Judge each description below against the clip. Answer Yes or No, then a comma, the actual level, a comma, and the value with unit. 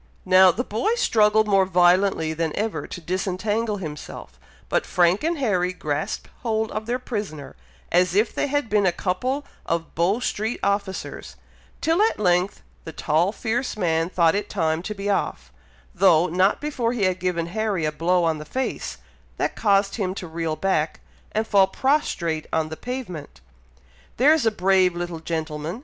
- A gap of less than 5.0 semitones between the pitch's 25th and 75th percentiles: Yes, average, 4.5 semitones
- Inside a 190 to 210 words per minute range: No, average, 170 wpm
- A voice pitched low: No, high, 190 Hz